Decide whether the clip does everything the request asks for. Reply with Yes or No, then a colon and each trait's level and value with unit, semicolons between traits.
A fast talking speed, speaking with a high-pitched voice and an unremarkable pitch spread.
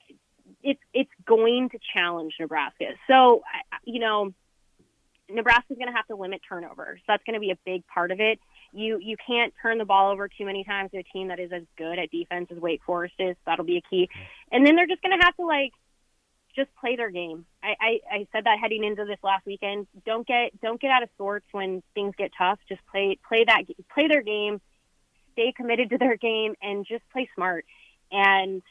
Yes: fast, 220 wpm; high, 205 Hz; average, 4.0 semitones